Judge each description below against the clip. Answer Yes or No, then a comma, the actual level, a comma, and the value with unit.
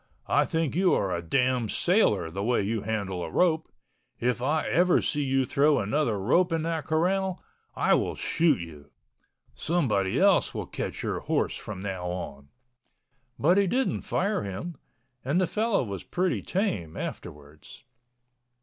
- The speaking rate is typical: Yes, average, 160 wpm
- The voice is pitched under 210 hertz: Yes, low, 135 Hz